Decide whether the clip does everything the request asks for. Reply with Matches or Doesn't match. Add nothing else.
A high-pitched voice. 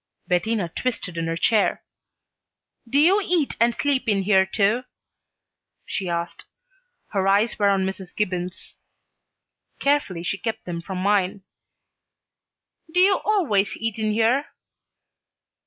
Matches